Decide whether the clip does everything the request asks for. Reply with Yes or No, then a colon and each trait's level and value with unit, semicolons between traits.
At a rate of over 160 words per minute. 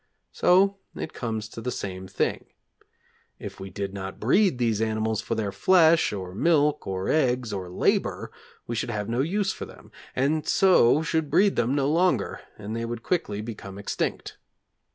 Yes: average, 175 wpm